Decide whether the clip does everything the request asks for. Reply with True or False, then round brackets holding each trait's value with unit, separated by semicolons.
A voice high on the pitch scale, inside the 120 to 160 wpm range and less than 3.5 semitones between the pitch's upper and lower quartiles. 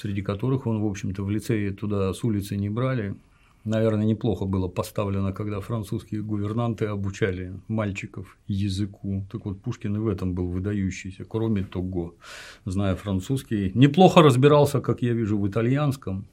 False (105 Hz; 150 wpm; 2.7 semitones)